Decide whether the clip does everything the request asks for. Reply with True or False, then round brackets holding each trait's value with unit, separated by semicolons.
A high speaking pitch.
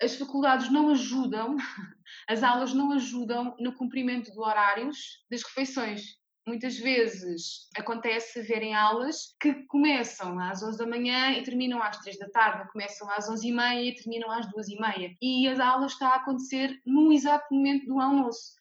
True (245 Hz)